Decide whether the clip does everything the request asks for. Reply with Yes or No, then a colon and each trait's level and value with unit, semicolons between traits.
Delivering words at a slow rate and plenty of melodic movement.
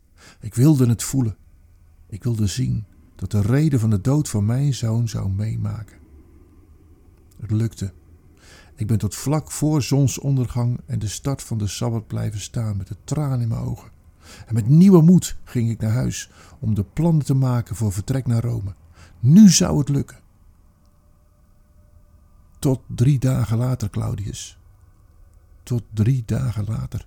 No: average, 155 wpm; wide, 5.9 semitones